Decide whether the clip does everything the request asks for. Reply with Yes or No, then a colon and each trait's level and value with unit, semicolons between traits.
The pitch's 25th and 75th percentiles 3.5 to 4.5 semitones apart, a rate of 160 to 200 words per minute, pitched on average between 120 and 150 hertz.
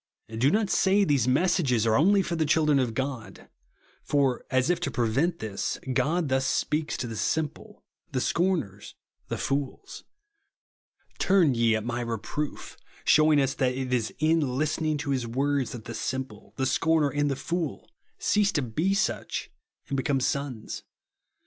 Yes: average, 4.2 semitones; average, 165 wpm; medium, 140 Hz